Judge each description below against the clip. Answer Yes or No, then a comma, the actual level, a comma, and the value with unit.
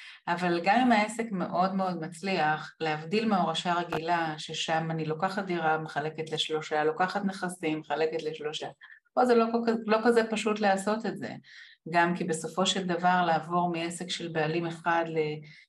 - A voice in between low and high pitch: Yes, medium, 175 Hz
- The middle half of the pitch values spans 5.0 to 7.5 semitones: No, average, 3.6 semitones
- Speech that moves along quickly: Yes, fast, 155 wpm